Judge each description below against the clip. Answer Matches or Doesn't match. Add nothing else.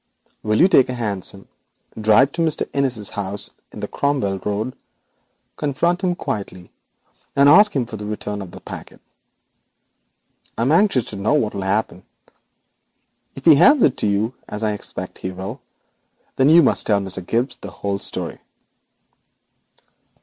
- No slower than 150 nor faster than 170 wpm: Matches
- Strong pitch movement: Matches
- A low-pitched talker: Matches